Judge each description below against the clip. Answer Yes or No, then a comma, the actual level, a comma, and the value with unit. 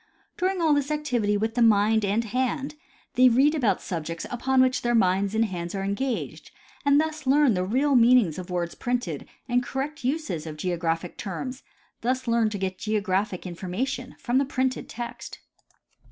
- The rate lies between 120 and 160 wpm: No, average, 175 wpm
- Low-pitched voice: No, high, 230 Hz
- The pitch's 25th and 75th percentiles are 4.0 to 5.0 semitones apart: No, wide, 5.6 semitones